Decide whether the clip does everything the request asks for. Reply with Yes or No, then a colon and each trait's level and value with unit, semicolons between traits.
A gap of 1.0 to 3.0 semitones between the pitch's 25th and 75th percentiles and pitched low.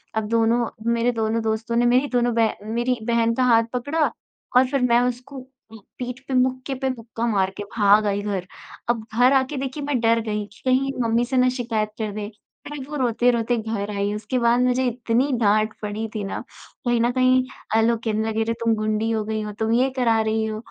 No: narrow, 2.4 semitones; high, 230 Hz